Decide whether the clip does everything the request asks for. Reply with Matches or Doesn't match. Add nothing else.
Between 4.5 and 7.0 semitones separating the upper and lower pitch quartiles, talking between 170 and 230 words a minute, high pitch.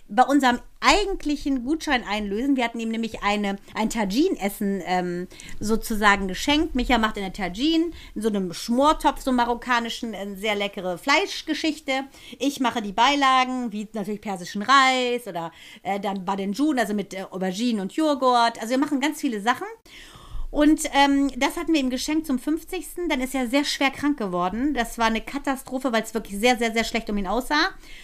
Matches